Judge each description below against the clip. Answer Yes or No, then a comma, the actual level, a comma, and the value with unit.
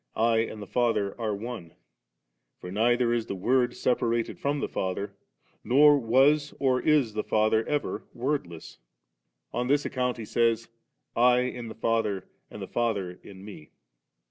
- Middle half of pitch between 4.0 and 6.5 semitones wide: No, average, 2.8 semitones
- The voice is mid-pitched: No, low, 115 Hz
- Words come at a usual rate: Yes, average, 165 wpm